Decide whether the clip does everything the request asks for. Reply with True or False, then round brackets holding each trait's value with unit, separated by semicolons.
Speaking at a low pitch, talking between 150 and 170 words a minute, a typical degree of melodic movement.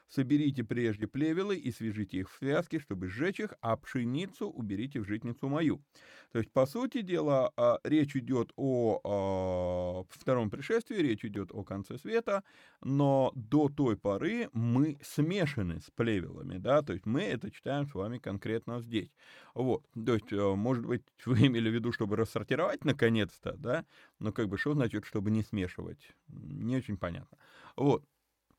True (120 Hz; 155 wpm; 4.9 semitones)